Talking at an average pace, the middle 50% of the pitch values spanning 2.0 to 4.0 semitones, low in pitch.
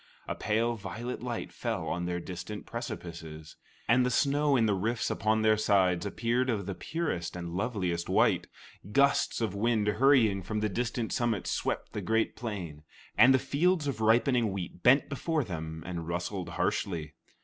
No: average, 170 wpm; average, 5.2 semitones; low, 110 Hz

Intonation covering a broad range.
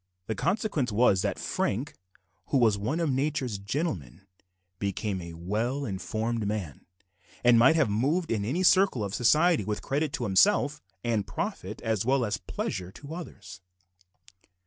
Yes: wide, 6.1 semitones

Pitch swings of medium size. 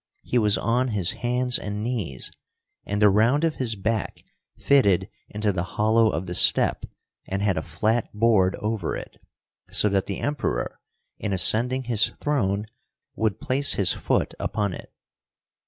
Yes: average, 3.5 semitones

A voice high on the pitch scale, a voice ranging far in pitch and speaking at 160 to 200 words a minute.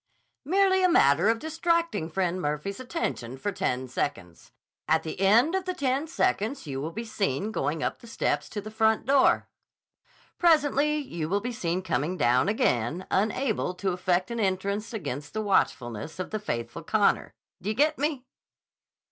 Yes: high, 200 Hz; wide, 8.5 semitones; average, 170 wpm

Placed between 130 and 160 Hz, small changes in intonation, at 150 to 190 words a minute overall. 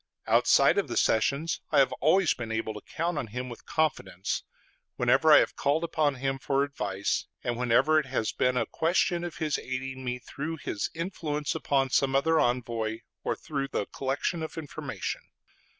No: low, 135 Hz; average, 4.2 semitones; average, 180 wpm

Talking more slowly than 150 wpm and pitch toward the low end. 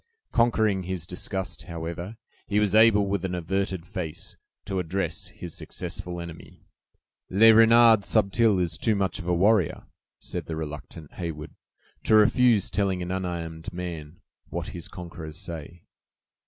Yes: average, 140 wpm; very low, 90 Hz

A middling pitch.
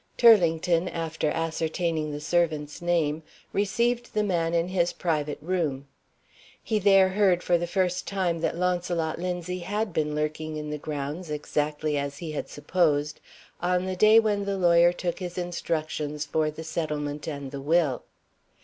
Yes: medium, 170 Hz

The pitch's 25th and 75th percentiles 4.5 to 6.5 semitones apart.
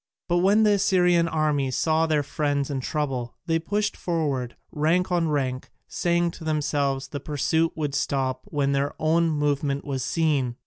No: average, 3.2 semitones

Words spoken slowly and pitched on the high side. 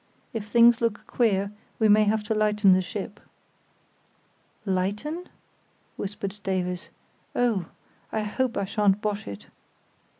Yes: slow, 125 wpm; high, 210 Hz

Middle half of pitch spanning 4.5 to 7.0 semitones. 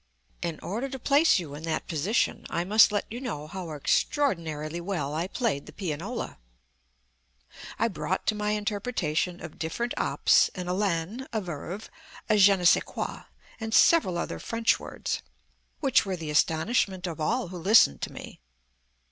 Yes: wide, 5.4 semitones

